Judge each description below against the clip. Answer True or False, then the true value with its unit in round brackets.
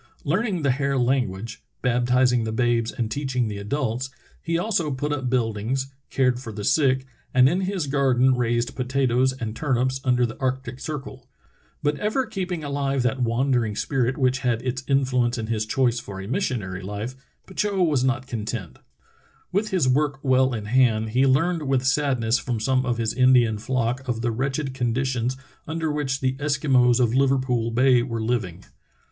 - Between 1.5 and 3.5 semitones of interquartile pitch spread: True (2.5 semitones)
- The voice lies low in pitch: True (130 Hz)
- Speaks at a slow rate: False (175 wpm)